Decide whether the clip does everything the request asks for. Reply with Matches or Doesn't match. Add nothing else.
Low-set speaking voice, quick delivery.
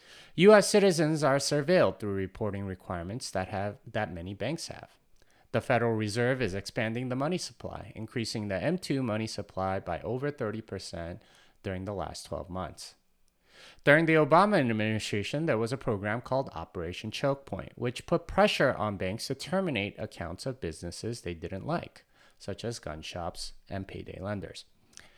Doesn't match